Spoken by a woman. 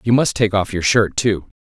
No: male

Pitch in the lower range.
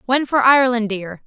No: high, 240 Hz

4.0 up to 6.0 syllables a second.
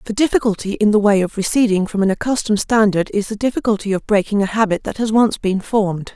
No: 6.3 syllables/s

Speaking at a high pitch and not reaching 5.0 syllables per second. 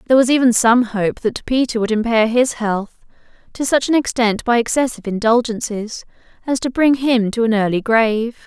No: high, 235 Hz; 5.3 syllables/s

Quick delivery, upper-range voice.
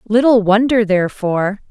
No: slow, 105 wpm; high, 210 Hz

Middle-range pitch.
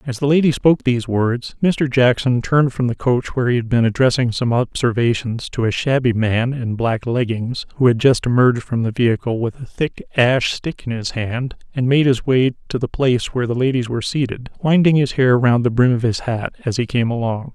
No: low, 125 Hz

